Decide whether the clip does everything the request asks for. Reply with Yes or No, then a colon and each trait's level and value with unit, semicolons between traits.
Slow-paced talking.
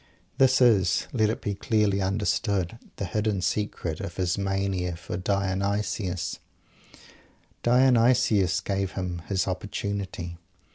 Yes: slow, 110 wpm